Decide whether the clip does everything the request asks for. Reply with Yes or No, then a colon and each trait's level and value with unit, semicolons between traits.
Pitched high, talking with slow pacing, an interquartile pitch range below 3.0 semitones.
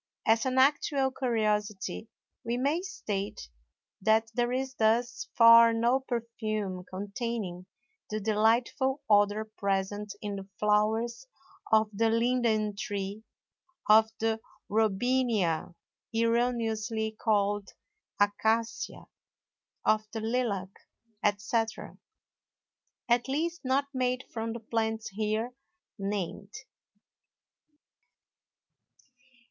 Yes: high, 220 Hz; slow, 90 wpm; narrow, 2.5 semitones